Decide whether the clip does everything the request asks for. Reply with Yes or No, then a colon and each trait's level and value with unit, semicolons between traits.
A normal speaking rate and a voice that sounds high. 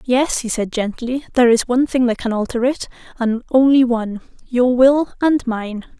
Yes: average, 180 wpm; high, 245 Hz